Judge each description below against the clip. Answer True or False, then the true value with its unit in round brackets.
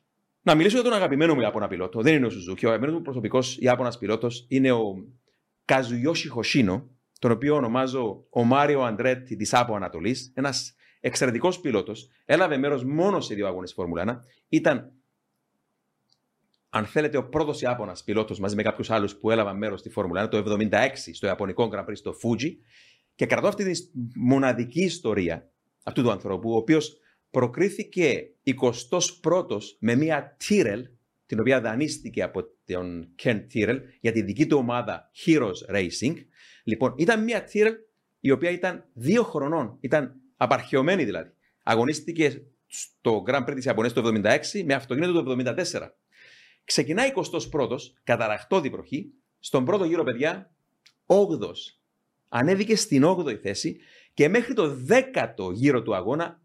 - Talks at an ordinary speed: True (150 wpm)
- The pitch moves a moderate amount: False (5.9 semitones)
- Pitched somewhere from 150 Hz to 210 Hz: False (130 Hz)